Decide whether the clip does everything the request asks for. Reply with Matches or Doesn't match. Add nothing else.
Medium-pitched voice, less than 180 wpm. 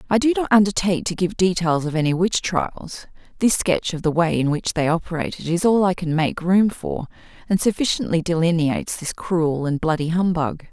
Doesn't match